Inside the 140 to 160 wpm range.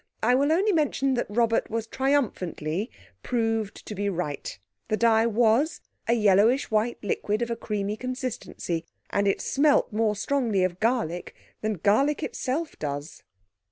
Yes: average, 150 wpm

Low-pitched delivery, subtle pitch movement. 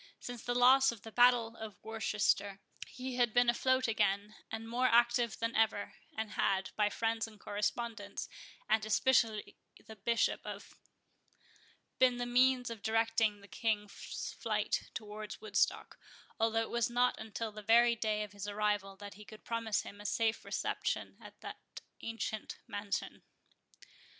No: high, 225 Hz; narrow, 2.3 semitones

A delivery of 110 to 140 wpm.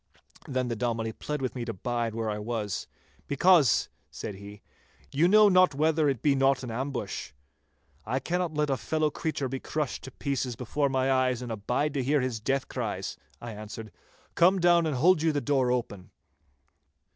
No: average, 185 wpm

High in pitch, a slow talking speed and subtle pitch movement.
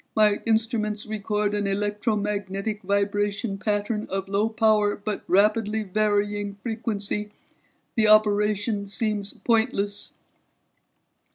Yes: high, 210 Hz; slow, 95 wpm; narrow, 1.0 semitones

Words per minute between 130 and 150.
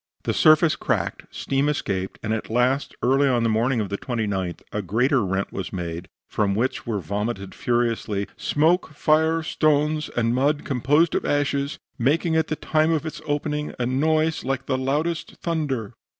No: average, 170 wpm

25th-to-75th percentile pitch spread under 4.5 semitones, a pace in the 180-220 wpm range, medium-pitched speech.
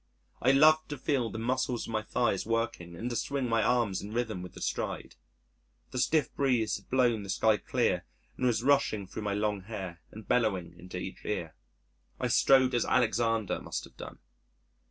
No: average, 3.6 semitones; average, 190 wpm; low, 115 Hz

